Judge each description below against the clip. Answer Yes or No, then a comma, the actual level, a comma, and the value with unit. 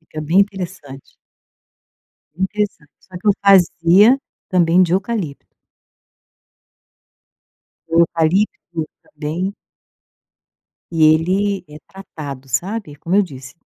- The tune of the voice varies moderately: Yes, average, 4.0 semitones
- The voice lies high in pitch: No, medium, 175 Hz